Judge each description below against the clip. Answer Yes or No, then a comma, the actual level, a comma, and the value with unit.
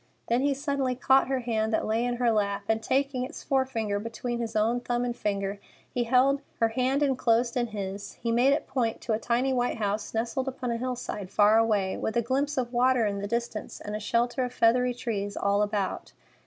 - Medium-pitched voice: No, high, 235 Hz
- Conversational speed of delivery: No, fast, 210 wpm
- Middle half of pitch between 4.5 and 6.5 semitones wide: No, average, 2.8 semitones